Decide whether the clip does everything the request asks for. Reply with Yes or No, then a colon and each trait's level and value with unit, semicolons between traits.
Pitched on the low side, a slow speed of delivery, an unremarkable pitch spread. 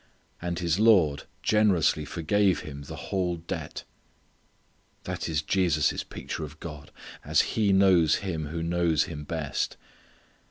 Yes: very low, 85 Hz; slow, 130 wpm; average, 3.6 semitones